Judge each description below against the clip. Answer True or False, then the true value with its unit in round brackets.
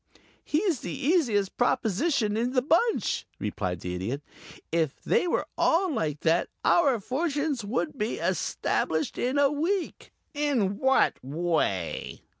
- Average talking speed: False (130 wpm)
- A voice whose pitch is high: True (245 Hz)